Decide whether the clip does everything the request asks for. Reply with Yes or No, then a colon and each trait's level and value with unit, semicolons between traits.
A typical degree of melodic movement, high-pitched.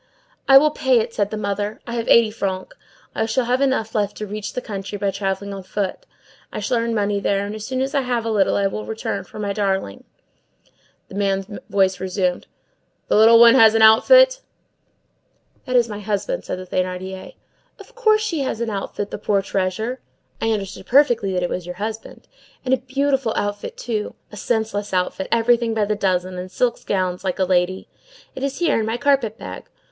Yes: average, 3.5 semitones; high, 215 Hz